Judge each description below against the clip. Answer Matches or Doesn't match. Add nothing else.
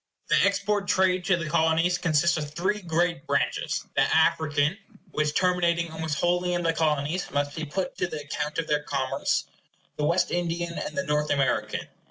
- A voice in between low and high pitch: Matches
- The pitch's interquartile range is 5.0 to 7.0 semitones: Doesn't match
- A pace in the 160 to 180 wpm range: Matches